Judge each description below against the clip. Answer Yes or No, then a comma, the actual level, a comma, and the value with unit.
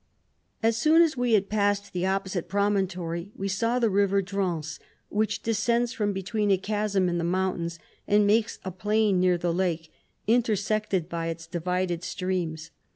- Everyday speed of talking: Yes, average, 165 wpm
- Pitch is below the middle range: No, high, 195 Hz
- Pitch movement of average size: Yes, average, 3.1 semitones